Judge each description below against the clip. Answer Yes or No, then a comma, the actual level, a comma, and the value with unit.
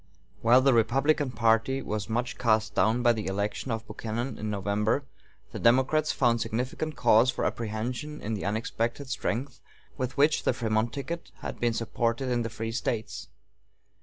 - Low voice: Yes, low, 115 Hz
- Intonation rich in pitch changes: No, average, 2.9 semitones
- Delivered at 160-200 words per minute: Yes, average, 165 wpm